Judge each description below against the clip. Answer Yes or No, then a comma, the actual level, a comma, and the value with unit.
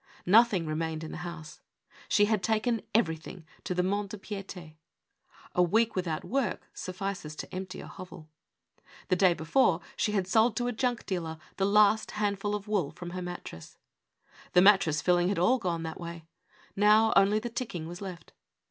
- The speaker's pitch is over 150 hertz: Yes, high, 190 Hz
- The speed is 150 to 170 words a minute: No, average, 185 wpm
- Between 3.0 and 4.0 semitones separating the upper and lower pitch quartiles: Yes, average, 3.6 semitones